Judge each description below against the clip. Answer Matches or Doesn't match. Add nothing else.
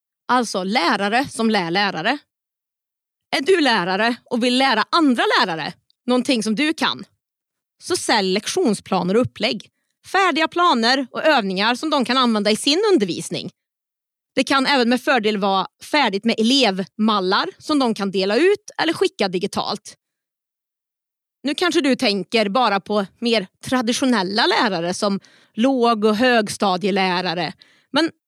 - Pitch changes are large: Matches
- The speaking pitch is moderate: Doesn't match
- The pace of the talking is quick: Doesn't match